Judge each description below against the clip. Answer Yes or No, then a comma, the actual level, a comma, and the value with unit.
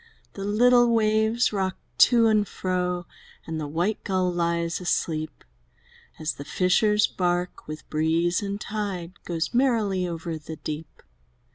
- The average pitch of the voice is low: No, medium, 180 Hz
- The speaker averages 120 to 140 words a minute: Yes, slow, 135 wpm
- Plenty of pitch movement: No, average, 4.0 semitones